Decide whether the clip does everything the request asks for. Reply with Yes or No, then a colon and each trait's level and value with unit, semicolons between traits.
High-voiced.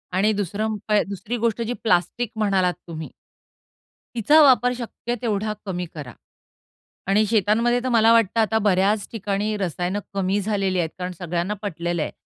Yes: high, 205 Hz